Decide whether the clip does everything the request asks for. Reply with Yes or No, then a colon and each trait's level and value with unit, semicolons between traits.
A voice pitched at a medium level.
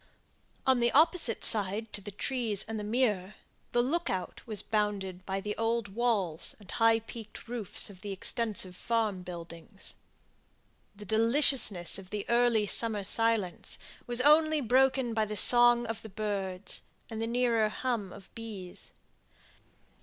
No: high, 220 Hz